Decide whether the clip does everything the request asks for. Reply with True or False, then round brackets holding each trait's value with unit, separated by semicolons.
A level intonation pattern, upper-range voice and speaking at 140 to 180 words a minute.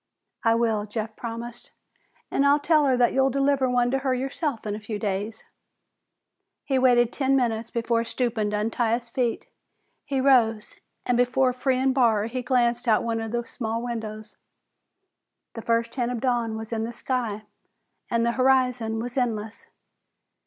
True (2.3 semitones; 235 Hz; 170 wpm)